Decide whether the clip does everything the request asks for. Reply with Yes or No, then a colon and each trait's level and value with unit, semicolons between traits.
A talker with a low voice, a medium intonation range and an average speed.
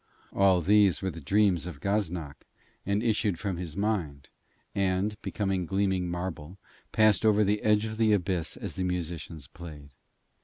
Yes: very low, 95 Hz; average, 3.3 semitones; average, 155 wpm